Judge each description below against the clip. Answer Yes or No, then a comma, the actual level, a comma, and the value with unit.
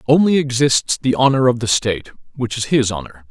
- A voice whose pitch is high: No, low, 125 Hz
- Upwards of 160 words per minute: Yes, average, 200 wpm